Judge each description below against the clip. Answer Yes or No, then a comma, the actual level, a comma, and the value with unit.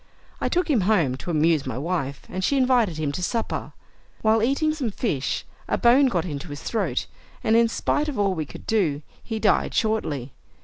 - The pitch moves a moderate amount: No, wide, 7.4 semitones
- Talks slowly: No, average, 200 wpm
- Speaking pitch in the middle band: No, high, 200 Hz